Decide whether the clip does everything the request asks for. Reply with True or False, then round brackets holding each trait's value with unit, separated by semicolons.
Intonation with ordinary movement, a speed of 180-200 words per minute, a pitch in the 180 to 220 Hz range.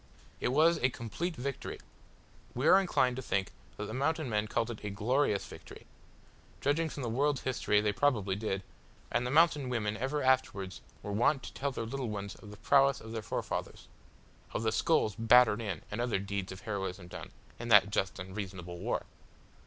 False (4.8 semitones; 190 wpm; 115 Hz)